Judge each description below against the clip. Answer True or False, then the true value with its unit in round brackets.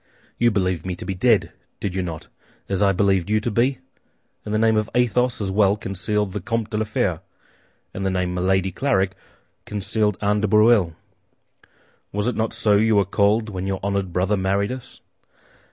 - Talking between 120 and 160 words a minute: False (190 wpm)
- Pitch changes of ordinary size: False (2.2 semitones)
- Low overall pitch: True (100 Hz)